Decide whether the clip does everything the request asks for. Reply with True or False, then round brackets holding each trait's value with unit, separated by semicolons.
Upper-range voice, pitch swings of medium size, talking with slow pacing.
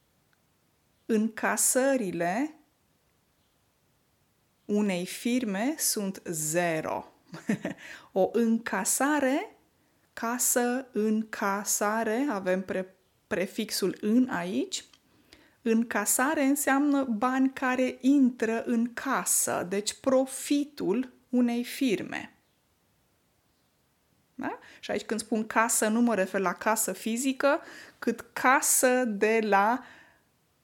True (230 Hz; 3.7 semitones; 80 wpm)